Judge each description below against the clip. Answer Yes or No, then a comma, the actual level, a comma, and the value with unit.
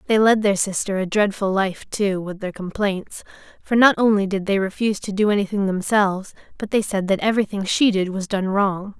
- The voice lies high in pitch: Yes, high, 200 Hz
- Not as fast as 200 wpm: No, fast, 205 wpm